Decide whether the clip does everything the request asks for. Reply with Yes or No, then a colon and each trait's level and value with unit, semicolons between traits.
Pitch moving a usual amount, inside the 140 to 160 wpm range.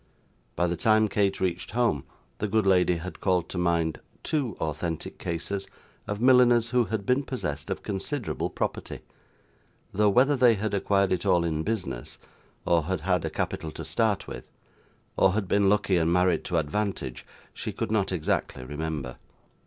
No: average, 4.5 semitones; average, 170 wpm